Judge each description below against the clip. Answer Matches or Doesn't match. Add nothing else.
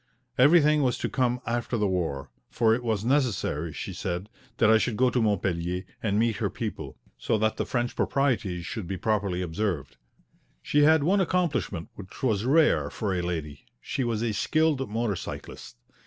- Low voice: Matches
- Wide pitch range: Matches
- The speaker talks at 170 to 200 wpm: Matches